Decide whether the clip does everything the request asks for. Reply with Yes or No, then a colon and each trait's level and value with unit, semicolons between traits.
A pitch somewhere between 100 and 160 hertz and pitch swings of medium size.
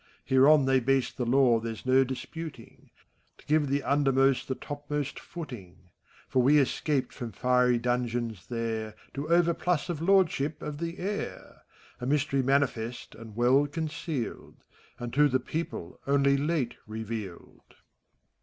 Yes: low, 135 Hz; average, 3.4 semitones